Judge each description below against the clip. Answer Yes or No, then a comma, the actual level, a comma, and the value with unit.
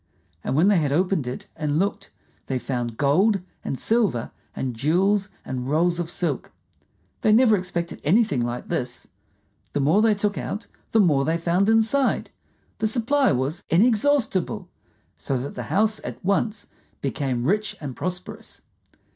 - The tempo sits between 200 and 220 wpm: No, average, 155 wpm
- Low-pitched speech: No, medium, 180 Hz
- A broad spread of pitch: Yes, wide, 7.2 semitones